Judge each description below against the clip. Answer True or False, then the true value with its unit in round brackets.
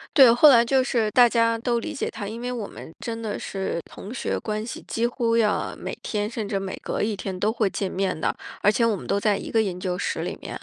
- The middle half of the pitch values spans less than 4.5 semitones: True (2.8 semitones)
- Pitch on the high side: True (220 Hz)